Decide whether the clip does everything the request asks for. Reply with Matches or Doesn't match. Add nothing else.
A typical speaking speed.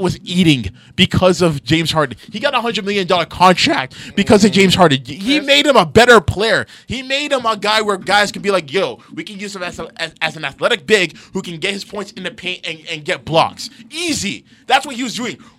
Doesn't match